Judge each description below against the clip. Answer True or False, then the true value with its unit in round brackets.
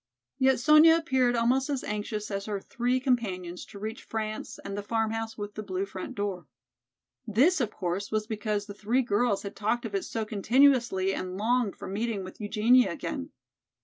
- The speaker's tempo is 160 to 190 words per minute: True (185 wpm)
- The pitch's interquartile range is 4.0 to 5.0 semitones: False (3.5 semitones)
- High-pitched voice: True (215 Hz)